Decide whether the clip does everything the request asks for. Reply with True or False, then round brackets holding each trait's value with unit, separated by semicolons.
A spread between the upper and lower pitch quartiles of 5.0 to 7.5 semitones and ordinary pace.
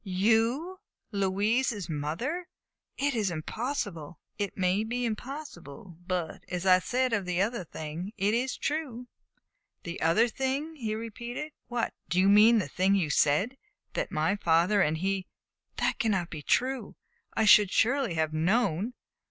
True (5.5 semitones; 150 wpm)